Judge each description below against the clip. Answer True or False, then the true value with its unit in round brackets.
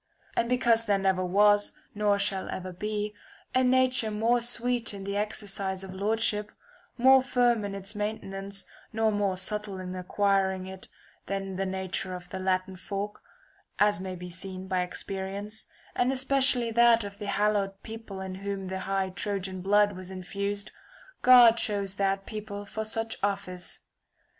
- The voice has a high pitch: True (200 Hz)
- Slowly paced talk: False (160 wpm)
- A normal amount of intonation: False (2.3 semitones)